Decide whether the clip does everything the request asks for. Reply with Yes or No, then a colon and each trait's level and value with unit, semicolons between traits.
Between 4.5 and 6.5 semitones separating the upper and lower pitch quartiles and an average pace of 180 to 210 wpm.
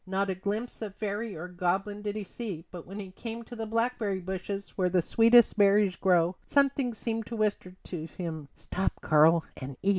No: average, 3.6 semitones; average, 200 wpm